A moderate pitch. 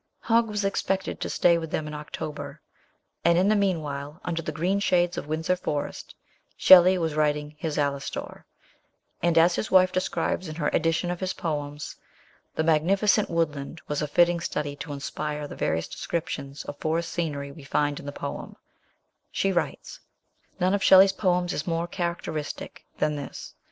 Yes: medium, 165 Hz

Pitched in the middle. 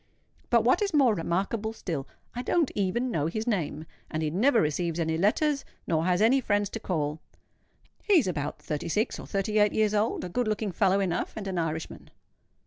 No: high, 200 Hz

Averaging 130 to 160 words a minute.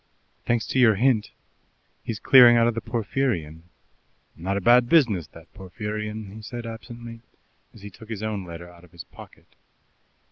No: average, 170 wpm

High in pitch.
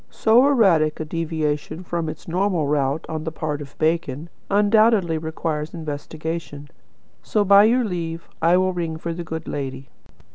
No: medium, 165 Hz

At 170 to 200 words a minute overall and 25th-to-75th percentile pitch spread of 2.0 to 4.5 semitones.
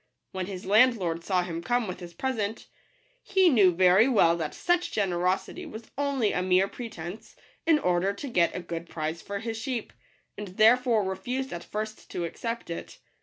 No: average, 180 wpm; average, 5.2 semitones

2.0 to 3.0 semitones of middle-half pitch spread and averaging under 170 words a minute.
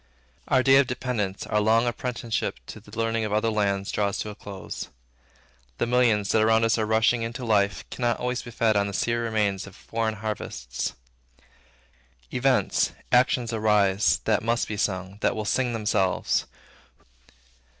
Yes: narrow, 2.4 semitones; average, 160 wpm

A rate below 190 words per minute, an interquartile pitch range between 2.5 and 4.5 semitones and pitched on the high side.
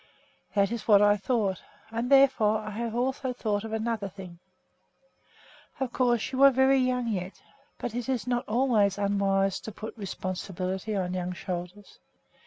Yes: average, 160 wpm; average, 3.9 semitones; high, 215 Hz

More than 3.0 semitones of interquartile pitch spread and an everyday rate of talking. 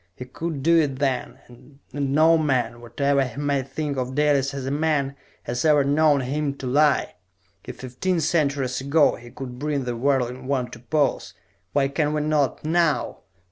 No: narrow, 2.6 semitones; average, 180 wpm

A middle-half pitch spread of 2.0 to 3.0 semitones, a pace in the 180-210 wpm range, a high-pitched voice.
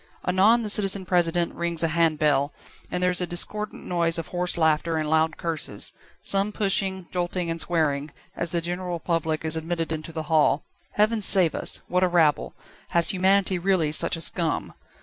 No: narrow, 2.5 semitones; average, 185 wpm; medium, 170 Hz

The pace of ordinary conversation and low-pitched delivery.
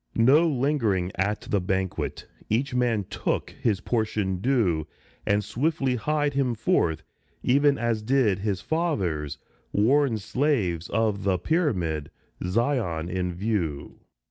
No: slow, 120 wpm; low, 110 Hz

